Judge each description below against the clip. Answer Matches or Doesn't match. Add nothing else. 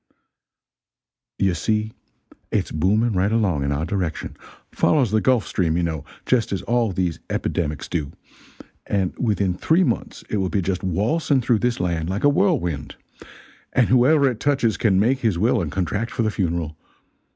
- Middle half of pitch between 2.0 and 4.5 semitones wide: Doesn't match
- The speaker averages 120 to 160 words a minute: Doesn't match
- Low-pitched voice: Matches